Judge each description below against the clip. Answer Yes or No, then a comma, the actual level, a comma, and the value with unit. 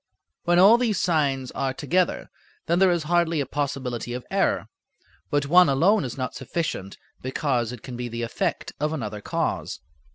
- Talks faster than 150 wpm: Yes, average, 170 wpm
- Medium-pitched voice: Yes, medium, 145 Hz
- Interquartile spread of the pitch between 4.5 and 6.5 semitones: Yes, wide, 5.5 semitones